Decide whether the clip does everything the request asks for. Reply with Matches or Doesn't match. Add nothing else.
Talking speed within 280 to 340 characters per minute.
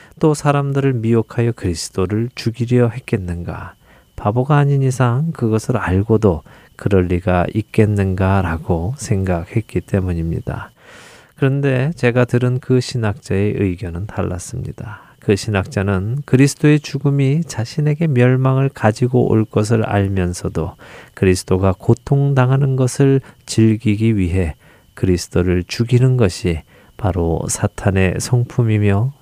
Matches